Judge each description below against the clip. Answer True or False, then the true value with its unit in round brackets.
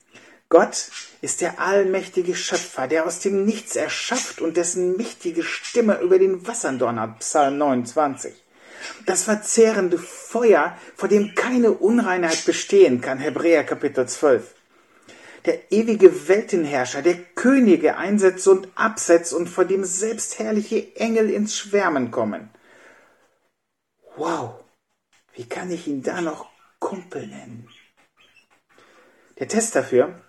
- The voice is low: False (190 Hz)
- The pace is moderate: False (120 wpm)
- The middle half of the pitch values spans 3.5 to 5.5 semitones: True (4.2 semitones)